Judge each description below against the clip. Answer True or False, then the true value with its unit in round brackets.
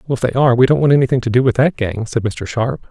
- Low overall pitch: True (125 Hz)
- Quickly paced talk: True (330 wpm)